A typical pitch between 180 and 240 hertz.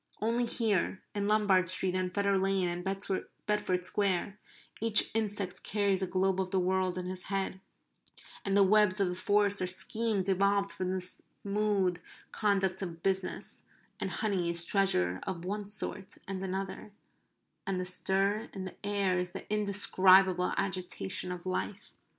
Yes: high, 190 Hz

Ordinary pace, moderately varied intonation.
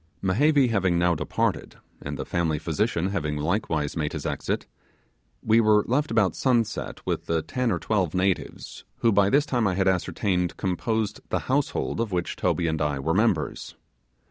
Yes: average, 170 wpm; average, 4.7 semitones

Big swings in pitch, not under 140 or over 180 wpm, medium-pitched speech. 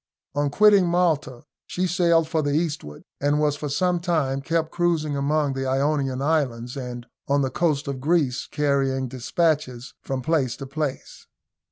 No: average, 3.4 semitones; average, 160 wpm; medium, 145 Hz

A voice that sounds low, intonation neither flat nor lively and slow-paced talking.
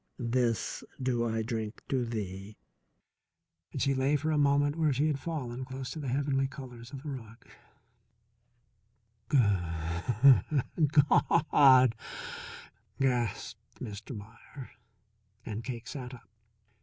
Yes: low, 130 Hz; average, 3.4 semitones; slow, 120 wpm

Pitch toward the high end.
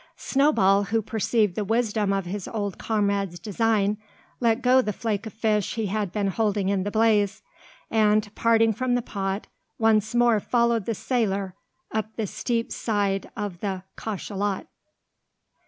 Yes: high, 215 Hz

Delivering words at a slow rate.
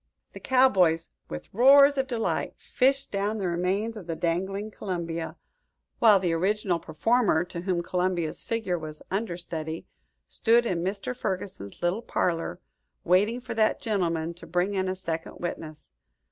No: average, 145 wpm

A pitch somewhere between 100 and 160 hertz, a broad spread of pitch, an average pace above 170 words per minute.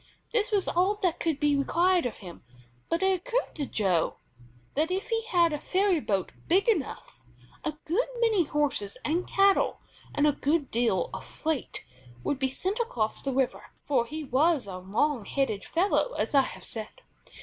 No: very high, 305 Hz; wide, 6.3 semitones; average, 180 wpm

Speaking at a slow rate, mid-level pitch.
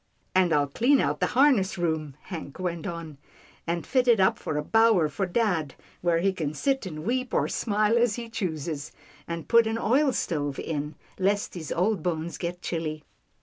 No: average, 195 wpm; medium, 180 Hz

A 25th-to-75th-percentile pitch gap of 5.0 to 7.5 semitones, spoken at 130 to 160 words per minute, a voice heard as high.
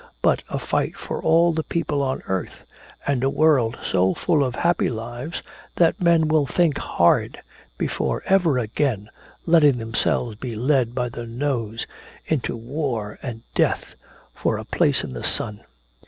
No: wide, 5.5 semitones; average, 155 wpm; low, 130 Hz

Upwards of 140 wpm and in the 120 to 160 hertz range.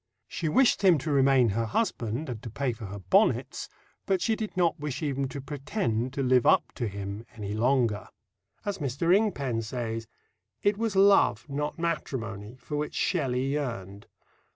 Yes: average, 170 wpm; low, 135 Hz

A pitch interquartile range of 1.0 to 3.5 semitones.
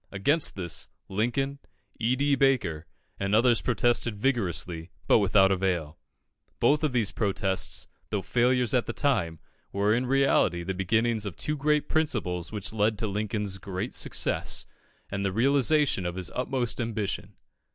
No: average, 4.9 semitones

